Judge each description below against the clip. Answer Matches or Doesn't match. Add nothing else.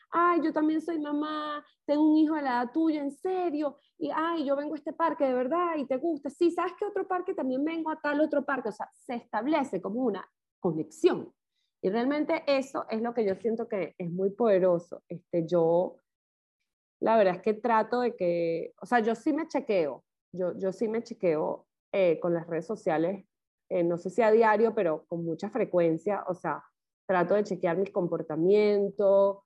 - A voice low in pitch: Doesn't match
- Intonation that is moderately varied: Doesn't match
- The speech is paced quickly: Matches